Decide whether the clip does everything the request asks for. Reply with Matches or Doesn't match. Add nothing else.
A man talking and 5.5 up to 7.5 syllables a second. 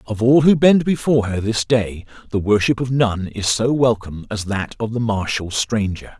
Doesn't match